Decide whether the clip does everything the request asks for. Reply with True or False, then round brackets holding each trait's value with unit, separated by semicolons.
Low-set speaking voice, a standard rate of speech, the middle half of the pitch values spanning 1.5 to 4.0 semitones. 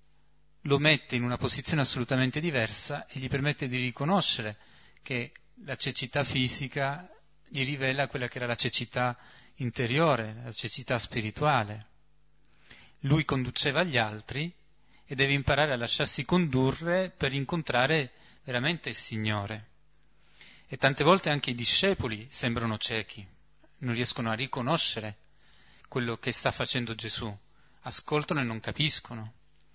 True (130 Hz; 125 wpm; 3.7 semitones)